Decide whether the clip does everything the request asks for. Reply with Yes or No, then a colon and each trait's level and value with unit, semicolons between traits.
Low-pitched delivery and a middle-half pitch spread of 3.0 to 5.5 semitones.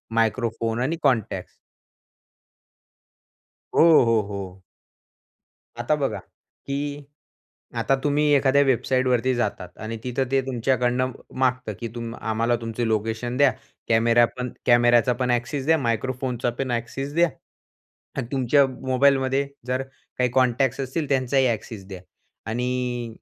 No: low, 125 Hz; narrow, 2.4 semitones